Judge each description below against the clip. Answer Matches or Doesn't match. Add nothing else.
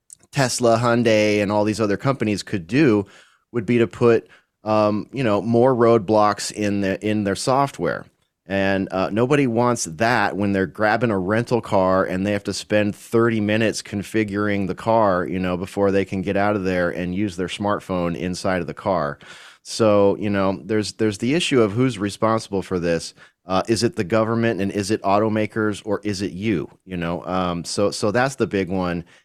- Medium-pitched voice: Doesn't match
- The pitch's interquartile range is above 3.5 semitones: Doesn't match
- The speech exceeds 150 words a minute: Matches